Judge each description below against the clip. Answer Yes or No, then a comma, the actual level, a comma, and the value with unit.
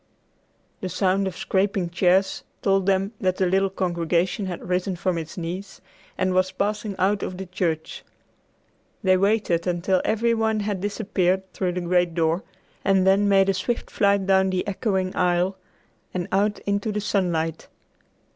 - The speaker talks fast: No, average, 160 wpm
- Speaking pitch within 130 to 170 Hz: No, high, 190 Hz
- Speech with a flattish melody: Yes, narrow, 1.7 semitones